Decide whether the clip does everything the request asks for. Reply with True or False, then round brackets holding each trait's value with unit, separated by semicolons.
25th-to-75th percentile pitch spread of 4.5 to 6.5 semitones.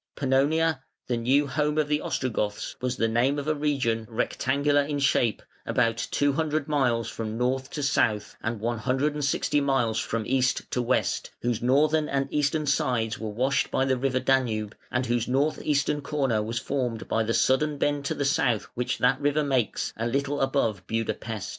False (3.7 semitones)